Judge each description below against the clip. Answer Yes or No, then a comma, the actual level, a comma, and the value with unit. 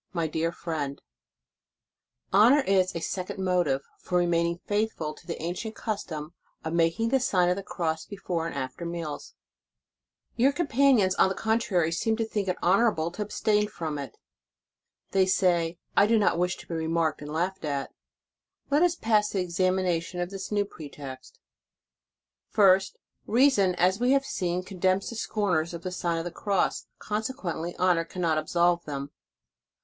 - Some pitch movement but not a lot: Yes, average, 3.8 semitones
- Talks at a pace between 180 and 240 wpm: No, average, 170 wpm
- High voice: No, medium, 180 Hz